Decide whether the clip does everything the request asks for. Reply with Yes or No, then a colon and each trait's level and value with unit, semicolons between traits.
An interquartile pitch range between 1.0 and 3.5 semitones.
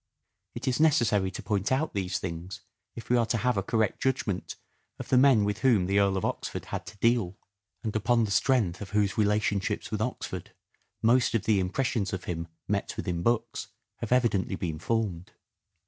No: average, 3.9 semitones